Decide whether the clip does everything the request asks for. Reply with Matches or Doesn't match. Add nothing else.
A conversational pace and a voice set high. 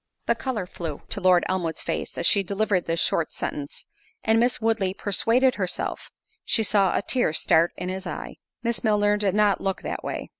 Matches